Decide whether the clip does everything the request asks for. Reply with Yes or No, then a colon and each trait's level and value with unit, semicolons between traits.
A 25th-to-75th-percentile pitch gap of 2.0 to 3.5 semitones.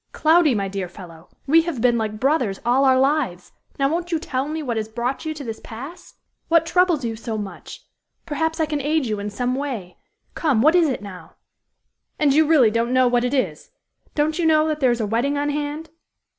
No: wide, 5.5 semitones